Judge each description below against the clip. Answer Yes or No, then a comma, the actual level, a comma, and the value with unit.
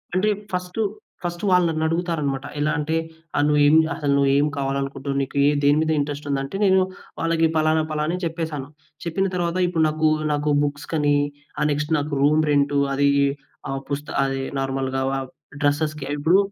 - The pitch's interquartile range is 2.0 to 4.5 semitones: Yes, narrow, 2.4 semitones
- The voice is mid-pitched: Yes, medium, 150 Hz